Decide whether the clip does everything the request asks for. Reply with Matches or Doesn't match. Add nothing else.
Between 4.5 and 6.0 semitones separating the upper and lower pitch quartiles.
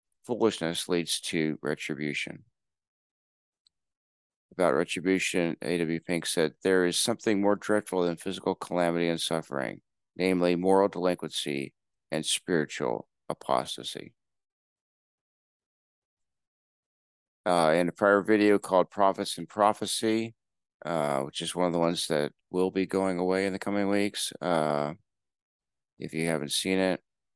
Doesn't match